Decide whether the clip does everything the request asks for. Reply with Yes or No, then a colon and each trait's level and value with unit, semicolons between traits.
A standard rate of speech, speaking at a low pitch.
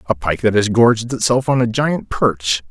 No: fast, 220 wpm; low, 115 Hz